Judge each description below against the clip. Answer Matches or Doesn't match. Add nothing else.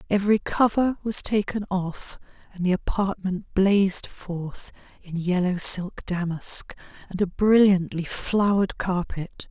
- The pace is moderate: Doesn't match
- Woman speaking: Matches